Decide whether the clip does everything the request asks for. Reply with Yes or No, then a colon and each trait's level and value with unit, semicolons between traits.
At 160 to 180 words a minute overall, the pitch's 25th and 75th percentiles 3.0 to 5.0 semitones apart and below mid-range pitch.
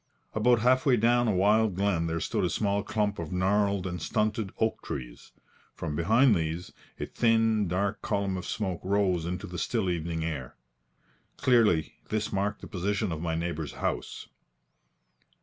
Yes: average, 165 wpm; average, 4.0 semitones; low, 100 Hz